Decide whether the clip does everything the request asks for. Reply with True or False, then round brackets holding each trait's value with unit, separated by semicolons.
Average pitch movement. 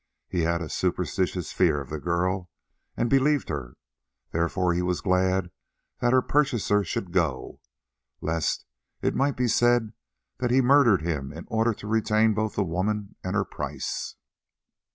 True (4.9 semitones)